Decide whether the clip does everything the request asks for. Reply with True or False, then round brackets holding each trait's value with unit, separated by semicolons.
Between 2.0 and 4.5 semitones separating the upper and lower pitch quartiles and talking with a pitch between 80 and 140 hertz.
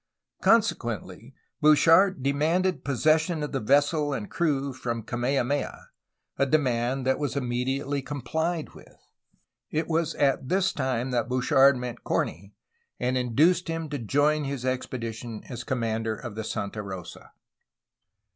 True (4.0 semitones; 135 Hz)